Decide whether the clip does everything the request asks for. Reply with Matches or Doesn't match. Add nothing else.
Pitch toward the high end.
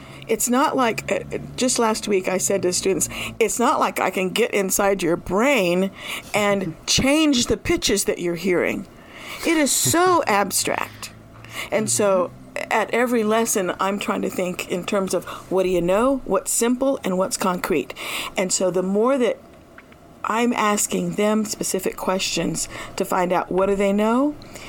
Matches